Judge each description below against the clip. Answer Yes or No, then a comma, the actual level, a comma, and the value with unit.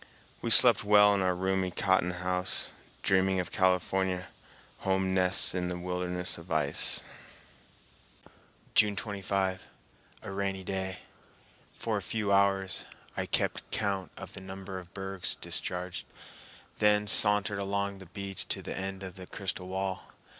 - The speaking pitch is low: Yes, very low, 95 Hz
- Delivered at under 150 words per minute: Yes, average, 140 wpm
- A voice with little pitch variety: Yes, narrow, 1.3 semitones